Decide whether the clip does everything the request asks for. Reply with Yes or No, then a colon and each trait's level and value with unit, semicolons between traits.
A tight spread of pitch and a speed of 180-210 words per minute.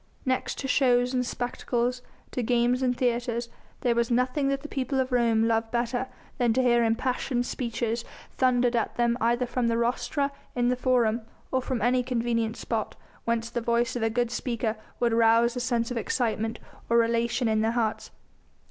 Yes: narrow, 1.3 semitones; average, 185 wpm